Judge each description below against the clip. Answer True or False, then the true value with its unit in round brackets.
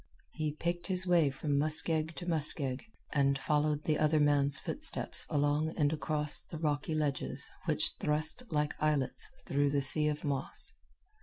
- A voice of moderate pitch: True (150 Hz)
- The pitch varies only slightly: True (1.5 semitones)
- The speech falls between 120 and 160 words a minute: True (155 wpm)